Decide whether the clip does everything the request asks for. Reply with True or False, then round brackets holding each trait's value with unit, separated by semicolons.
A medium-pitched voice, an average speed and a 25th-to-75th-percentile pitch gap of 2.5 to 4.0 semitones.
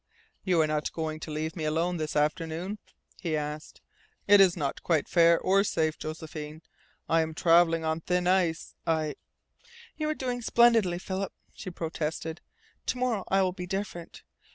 True (165 Hz; 170 wpm; 3.2 semitones)